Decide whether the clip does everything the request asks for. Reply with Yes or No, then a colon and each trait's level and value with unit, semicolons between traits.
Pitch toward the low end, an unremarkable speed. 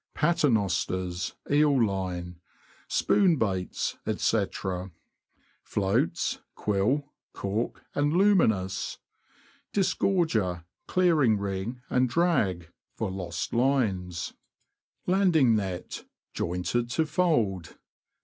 No: low, 110 Hz; slow, 80 wpm